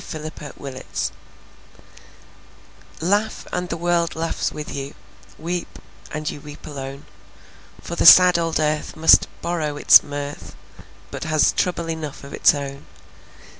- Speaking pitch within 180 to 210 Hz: No, medium, 155 Hz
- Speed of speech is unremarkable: Yes, average, 145 wpm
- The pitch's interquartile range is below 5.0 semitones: Yes, average, 2.9 semitones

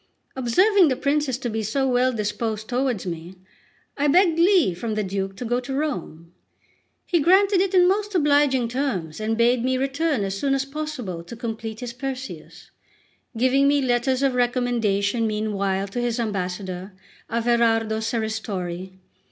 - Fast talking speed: No, average, 155 wpm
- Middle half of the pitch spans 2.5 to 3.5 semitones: No, average, 4.5 semitones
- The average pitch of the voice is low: No, high, 240 Hz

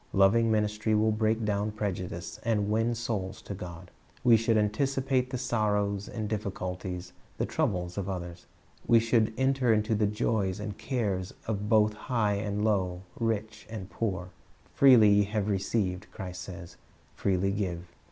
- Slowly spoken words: No, average, 150 wpm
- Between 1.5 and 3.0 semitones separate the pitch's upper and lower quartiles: Yes, average, 2.7 semitones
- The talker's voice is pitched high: No, low, 105 Hz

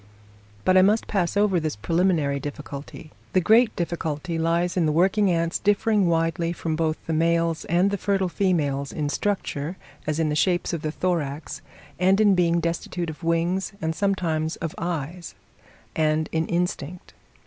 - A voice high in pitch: No, medium, 170 Hz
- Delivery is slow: No, average, 165 wpm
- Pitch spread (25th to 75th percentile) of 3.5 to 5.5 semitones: No, average, 2.7 semitones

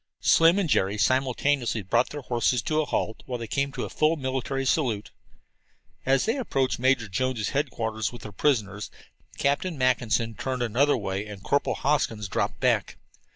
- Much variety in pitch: No, average, 4.1 semitones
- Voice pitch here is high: No, low, 130 Hz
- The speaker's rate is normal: Yes, average, 165 wpm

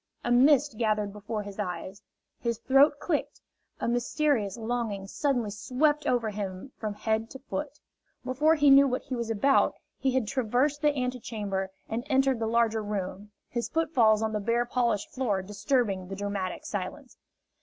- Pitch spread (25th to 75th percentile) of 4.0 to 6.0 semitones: Yes, average, 4.3 semitones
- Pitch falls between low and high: No, high, 235 Hz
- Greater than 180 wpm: No, average, 165 wpm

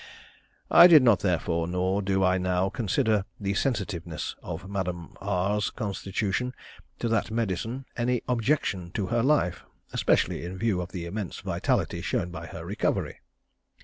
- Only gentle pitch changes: No, average, 4.1 semitones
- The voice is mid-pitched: No, low, 100 Hz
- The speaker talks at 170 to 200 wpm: No, average, 145 wpm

